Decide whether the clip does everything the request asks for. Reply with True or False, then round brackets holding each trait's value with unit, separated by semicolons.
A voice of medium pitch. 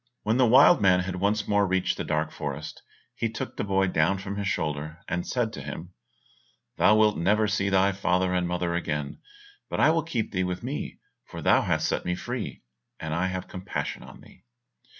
False (95 Hz)